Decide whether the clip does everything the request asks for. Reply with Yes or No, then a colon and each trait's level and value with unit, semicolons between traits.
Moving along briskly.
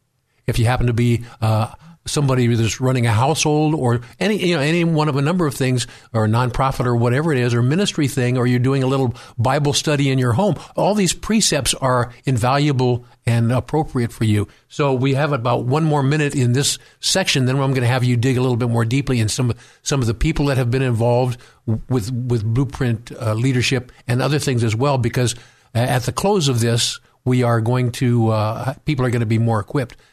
Yes: fast, 225 wpm